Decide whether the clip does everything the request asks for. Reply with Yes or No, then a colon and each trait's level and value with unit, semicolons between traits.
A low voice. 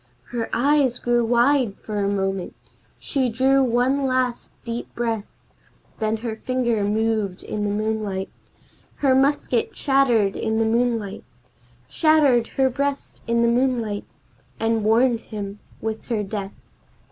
No: high, 235 Hz